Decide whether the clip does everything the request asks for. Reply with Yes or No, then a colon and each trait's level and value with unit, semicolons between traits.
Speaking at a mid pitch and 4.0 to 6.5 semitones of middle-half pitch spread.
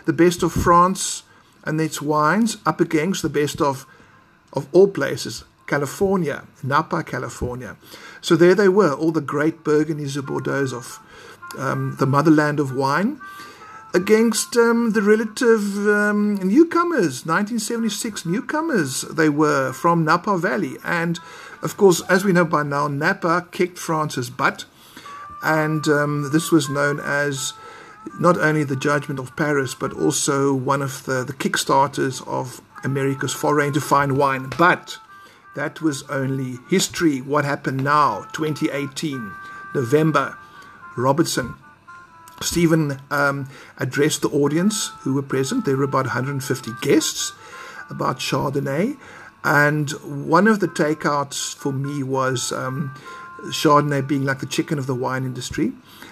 Yes: medium, 155 Hz; average, 4.9 semitones